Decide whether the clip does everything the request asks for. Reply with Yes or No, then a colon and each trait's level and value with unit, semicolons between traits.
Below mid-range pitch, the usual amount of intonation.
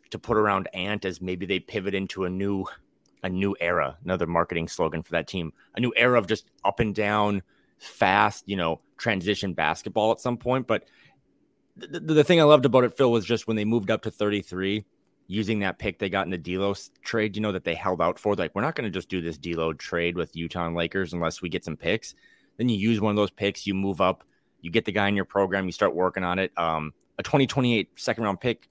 Yes: low, 100 Hz; average, 3.5 semitones